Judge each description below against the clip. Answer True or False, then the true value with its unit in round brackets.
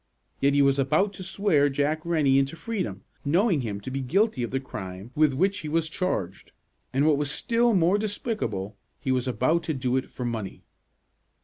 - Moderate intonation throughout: False (5.8 semitones)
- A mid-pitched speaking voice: True (145 Hz)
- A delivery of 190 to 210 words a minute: True (195 wpm)